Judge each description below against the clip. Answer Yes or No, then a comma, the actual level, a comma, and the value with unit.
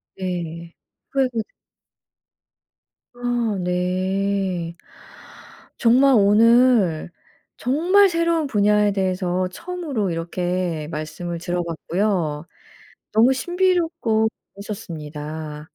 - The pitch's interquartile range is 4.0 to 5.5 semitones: No, wide, 6.0 semitones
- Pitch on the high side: Yes, high, 195 Hz